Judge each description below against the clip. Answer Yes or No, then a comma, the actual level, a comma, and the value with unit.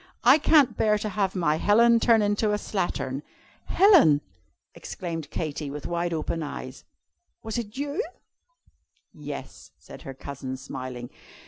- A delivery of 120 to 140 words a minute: Yes, slow, 135 wpm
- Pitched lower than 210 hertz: Yes, medium, 185 Hz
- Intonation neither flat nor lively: No, wide, 7.4 semitones